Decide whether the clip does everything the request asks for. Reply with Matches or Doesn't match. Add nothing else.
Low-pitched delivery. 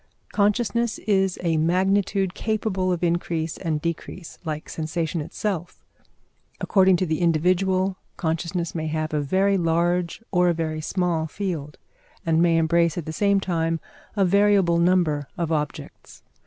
Doesn't match